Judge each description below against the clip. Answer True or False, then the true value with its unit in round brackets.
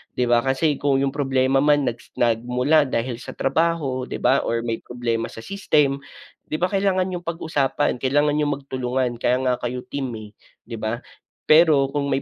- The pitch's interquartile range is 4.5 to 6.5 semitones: False (3.2 semitones)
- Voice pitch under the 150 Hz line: True (135 Hz)